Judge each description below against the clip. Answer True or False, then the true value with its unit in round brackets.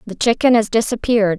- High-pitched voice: True (220 Hz)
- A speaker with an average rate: True (175 wpm)